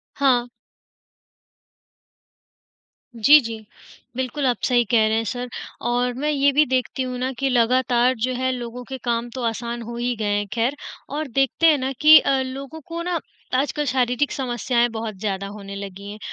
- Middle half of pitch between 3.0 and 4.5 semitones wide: No, narrow, 2.5 semitones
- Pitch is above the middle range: Yes, very high, 250 Hz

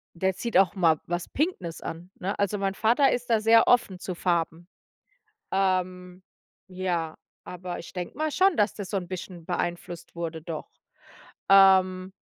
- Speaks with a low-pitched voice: No, medium, 185 Hz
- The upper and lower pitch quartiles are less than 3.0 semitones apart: Yes, narrow, 2.5 semitones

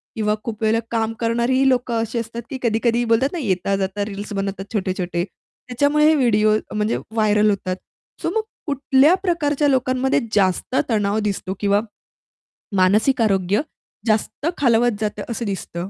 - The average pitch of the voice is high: Yes, high, 225 Hz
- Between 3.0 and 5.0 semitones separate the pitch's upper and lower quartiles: Yes, average, 3.9 semitones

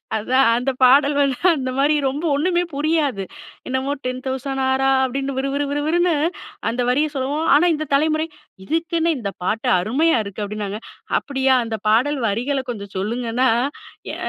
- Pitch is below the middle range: No, very high, 270 Hz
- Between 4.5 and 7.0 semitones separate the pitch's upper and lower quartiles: No, average, 3.3 semitones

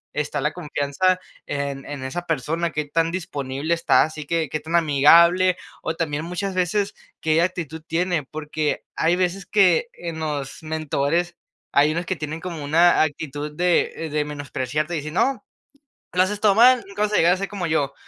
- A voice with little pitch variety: No, average, 3.1 semitones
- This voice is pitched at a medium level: Yes, medium, 160 Hz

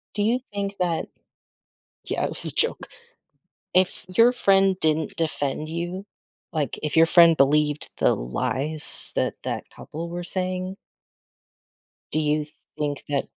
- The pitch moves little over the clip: No, average, 3.7 semitones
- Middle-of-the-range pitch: Yes, medium, 165 Hz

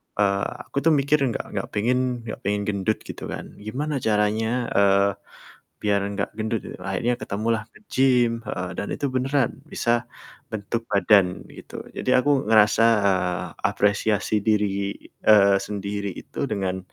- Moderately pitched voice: No, low, 105 Hz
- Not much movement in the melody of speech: No, average, 3.1 semitones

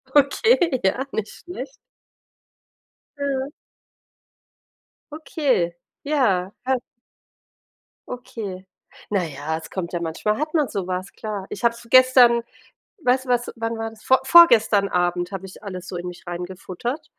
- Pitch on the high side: Yes, high, 225 Hz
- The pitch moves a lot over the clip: Yes, wide, 6.2 semitones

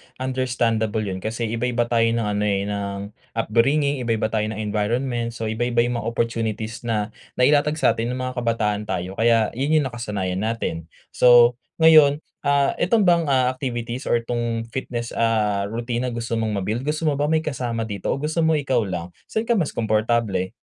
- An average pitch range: Yes, average, 3.0 semitones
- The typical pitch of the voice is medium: No, low, 115 Hz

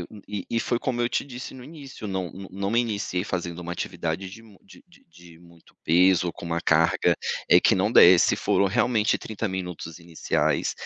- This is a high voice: No, very low, 95 Hz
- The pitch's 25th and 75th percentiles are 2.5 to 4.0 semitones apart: No, average, 4.6 semitones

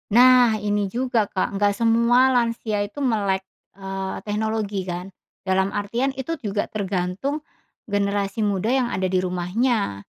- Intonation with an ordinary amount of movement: Yes, average, 3.4 semitones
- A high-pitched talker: Yes, high, 205 Hz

